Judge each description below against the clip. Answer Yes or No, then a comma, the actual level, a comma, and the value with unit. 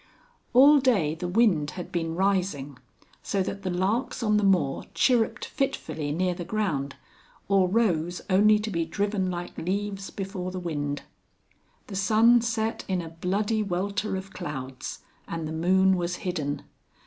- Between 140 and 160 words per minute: Yes, average, 155 wpm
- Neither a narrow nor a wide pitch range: Yes, average, 3.9 semitones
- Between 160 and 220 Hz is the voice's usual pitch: Yes, medium, 185 Hz